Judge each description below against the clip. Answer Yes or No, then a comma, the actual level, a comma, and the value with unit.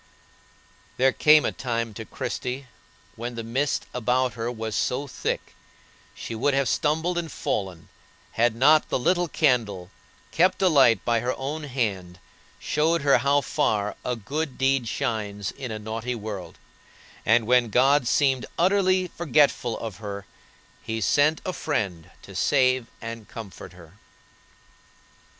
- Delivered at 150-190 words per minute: No, average, 140 wpm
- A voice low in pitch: Yes, low, 125 Hz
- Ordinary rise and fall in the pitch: Yes, average, 4.5 semitones